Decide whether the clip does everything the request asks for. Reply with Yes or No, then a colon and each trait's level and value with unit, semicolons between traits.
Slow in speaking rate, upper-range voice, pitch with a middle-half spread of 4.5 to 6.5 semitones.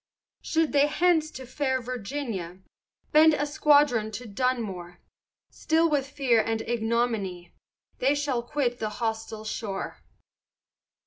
Yes: slow, 120 wpm; high, 245 Hz; average, 4.9 semitones